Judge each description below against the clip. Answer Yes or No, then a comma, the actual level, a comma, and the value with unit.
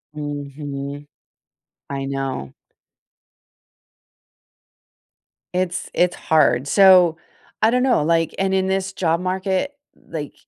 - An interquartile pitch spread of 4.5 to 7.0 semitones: Yes, average, 4.8 semitones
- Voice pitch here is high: No, medium, 165 Hz